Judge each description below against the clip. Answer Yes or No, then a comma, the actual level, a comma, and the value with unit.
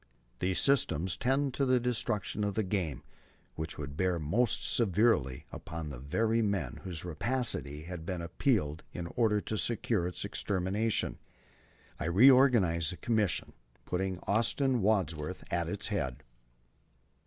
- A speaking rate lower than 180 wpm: Yes, average, 140 wpm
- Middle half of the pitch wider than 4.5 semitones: Yes, wide, 5.6 semitones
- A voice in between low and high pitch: No, very low, 95 Hz